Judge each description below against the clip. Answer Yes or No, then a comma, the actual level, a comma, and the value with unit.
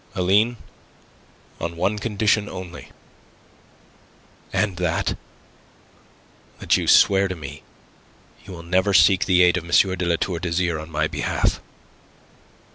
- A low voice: Yes, very low, 90 Hz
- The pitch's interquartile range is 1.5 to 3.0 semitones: Yes, narrow, 2.5 semitones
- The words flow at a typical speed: No, slow, 125 wpm